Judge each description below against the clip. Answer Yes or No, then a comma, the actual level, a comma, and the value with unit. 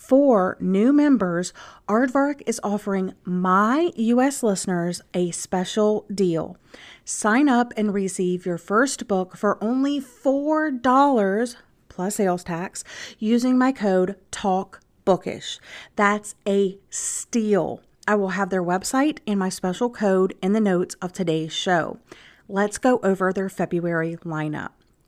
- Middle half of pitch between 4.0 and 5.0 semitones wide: Yes, average, 4.5 semitones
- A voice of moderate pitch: No, high, 200 Hz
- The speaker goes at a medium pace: No, slow, 125 wpm